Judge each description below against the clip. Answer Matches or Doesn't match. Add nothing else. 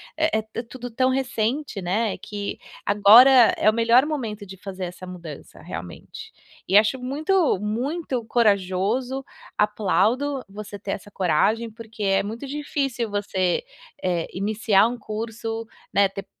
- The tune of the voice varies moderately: Matches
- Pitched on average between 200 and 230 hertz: Matches